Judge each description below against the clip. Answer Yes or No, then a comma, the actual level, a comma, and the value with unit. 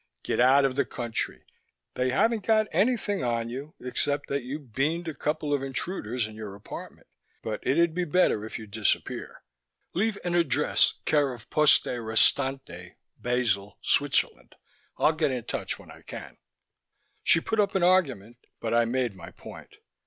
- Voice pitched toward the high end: No, low, 135 Hz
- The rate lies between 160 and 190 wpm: Yes, average, 165 wpm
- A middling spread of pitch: No, wide, 6.0 semitones